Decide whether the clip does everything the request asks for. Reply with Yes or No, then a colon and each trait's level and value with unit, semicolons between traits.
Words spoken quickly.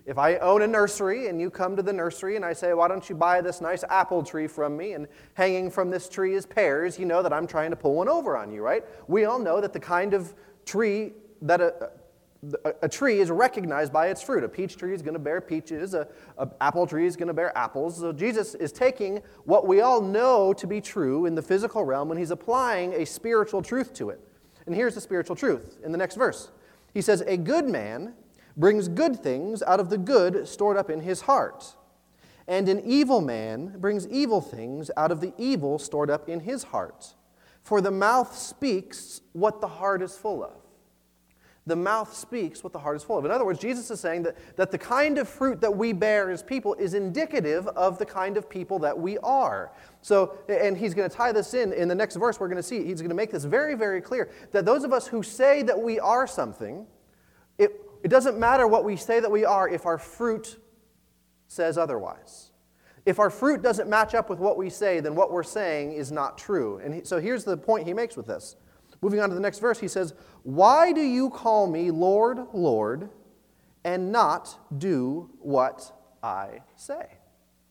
Yes: fast, 220 wpm